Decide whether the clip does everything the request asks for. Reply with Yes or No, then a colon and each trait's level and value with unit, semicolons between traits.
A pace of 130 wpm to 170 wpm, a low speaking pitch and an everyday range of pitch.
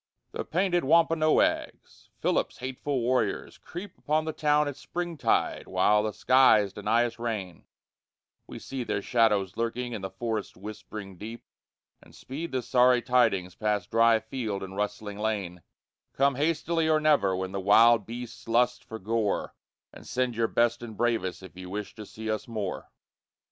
Yes: average, 160 wpm; low, 115 Hz; average, 3.9 semitones